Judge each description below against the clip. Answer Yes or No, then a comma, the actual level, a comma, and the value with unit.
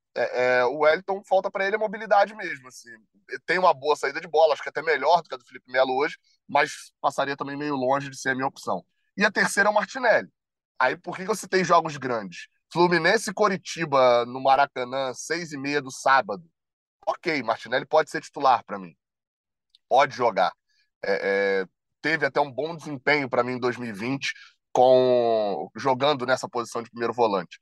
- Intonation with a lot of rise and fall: Yes, wide, 5.9 semitones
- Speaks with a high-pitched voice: No, medium, 140 Hz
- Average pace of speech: No, fast, 195 wpm